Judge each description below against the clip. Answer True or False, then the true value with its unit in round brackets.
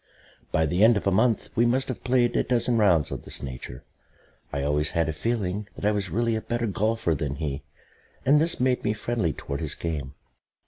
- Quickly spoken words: True (215 wpm)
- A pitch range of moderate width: False (7.2 semitones)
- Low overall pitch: True (105 Hz)